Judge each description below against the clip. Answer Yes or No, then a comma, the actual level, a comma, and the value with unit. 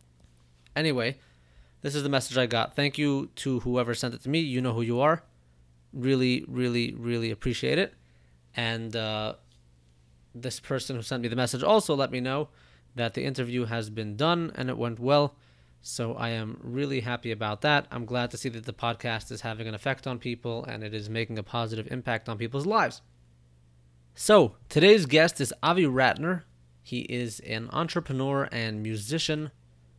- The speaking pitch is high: No, low, 120 Hz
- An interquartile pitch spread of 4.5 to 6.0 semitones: Yes, average, 4.8 semitones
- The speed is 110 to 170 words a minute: No, average, 180 wpm